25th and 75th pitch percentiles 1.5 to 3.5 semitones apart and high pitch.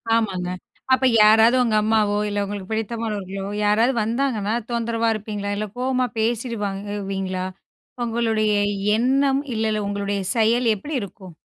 Yes: narrow, 2.4 semitones; high, 215 Hz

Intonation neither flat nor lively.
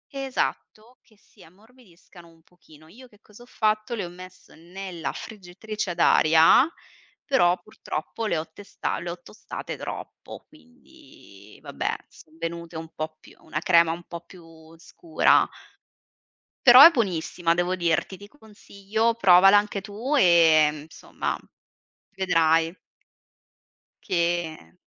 Yes: average, 4.7 semitones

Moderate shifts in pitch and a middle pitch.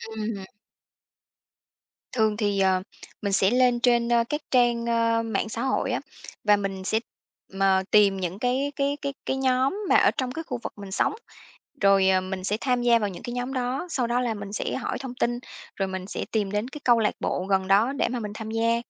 No: average, 4.0 semitones; high, 230 Hz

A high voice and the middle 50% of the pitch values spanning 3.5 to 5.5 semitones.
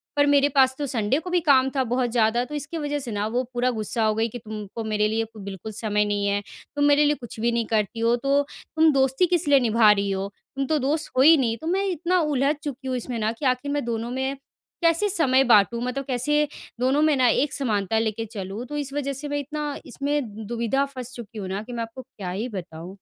Yes: very high, 250 Hz; average, 4.6 semitones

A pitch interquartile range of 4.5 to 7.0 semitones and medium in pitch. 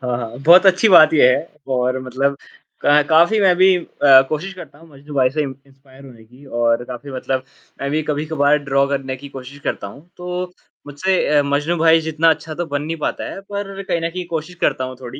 No: average, 3.9 semitones; medium, 145 Hz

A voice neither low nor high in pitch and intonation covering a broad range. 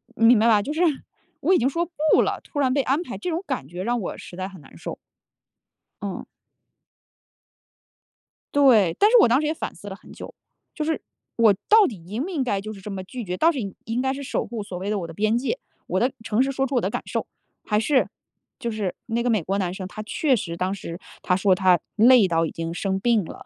No: high, 215 Hz; wide, 5.7 semitones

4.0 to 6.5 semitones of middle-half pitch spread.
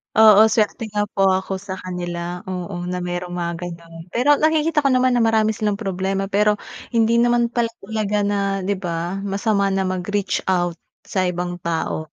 No: average, 3.5 semitones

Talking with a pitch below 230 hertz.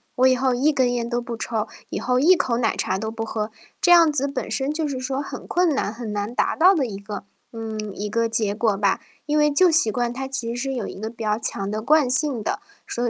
No: high, 240 Hz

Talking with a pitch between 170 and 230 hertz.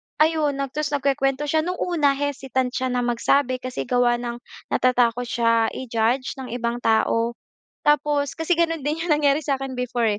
No: very high, 265 Hz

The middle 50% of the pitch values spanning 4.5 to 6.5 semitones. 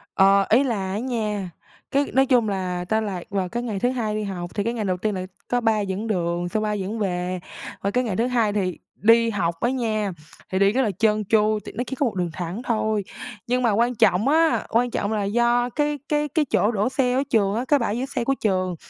No: average, 3.7 semitones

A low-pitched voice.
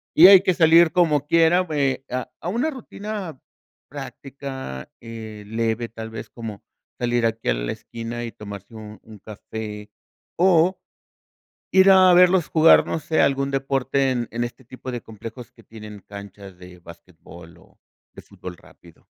Yes: low, 120 Hz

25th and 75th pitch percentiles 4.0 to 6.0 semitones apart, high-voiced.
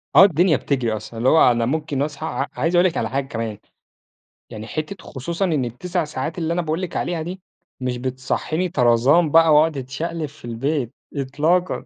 No: average, 4.5 semitones; medium, 150 Hz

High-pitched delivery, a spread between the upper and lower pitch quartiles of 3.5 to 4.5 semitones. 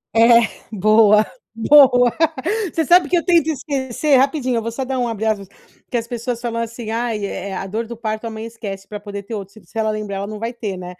No: high, 230 Hz; average, 2.7 semitones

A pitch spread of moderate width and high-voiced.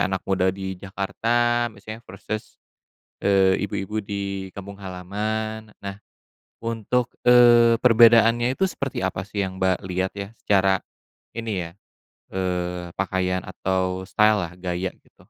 No: average, 3.1 semitones; low, 100 Hz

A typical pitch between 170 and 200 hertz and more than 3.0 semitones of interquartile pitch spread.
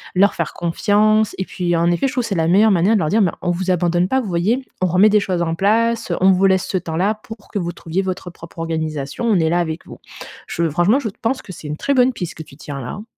Yes: medium, 185 Hz; average, 4.1 semitones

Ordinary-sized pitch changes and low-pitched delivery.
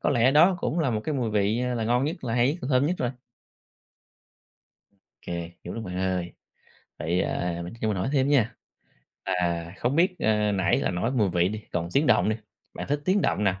No: wide, 6.7 semitones; low, 110 Hz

